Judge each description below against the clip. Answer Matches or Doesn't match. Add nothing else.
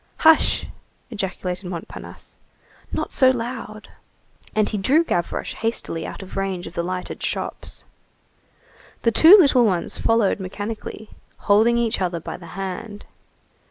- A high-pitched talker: Matches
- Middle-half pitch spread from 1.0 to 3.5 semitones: Doesn't match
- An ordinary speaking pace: Doesn't match